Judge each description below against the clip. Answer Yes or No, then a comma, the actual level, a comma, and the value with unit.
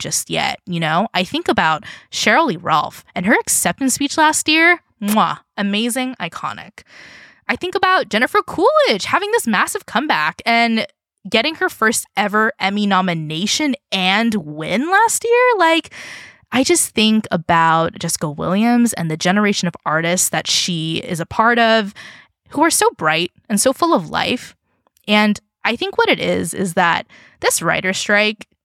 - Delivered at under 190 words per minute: Yes, average, 160 wpm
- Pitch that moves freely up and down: Yes, wide, 8.8 semitones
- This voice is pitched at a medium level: No, high, 220 Hz